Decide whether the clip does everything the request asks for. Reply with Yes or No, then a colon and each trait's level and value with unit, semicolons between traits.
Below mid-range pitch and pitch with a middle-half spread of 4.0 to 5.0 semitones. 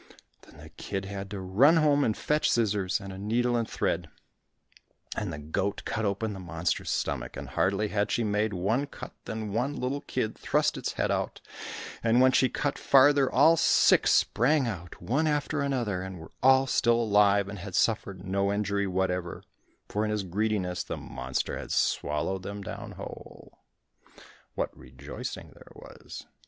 Yes: low, 105 Hz; average, 4.6 semitones